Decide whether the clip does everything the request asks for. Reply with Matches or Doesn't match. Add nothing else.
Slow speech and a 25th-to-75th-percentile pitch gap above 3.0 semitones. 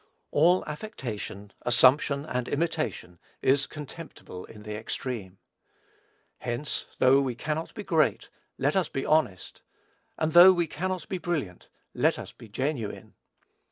Matches